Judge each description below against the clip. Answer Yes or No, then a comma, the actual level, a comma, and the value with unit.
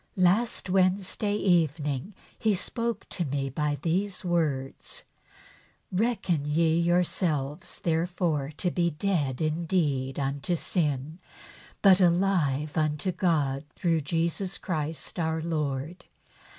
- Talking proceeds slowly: Yes, slow, 110 wpm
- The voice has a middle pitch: Yes, medium, 165 Hz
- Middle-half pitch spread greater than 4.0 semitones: No, average, 3.7 semitones